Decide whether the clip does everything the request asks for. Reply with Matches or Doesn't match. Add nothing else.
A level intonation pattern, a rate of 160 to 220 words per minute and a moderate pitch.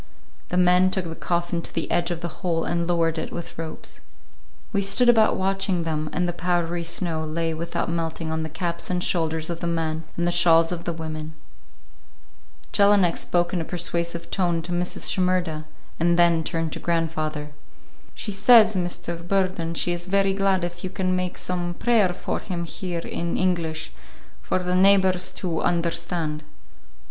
Matches